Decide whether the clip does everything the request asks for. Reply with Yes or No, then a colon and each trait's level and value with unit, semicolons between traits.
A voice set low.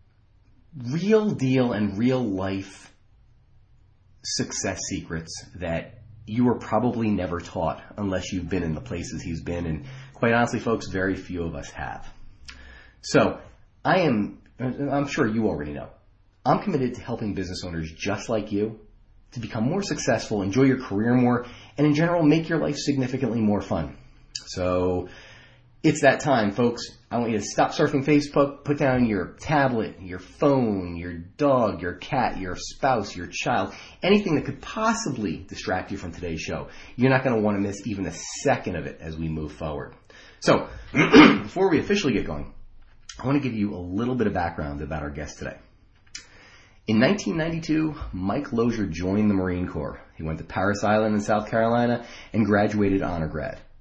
Yes: low, 105 Hz